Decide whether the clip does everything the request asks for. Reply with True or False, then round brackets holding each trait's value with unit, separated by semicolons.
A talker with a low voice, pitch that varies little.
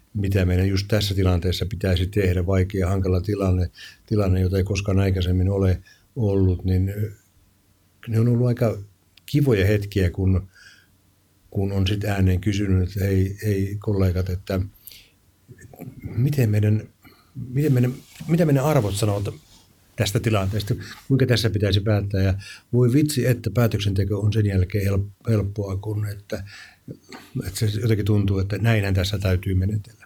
True (100 Hz; 2.3 semitones)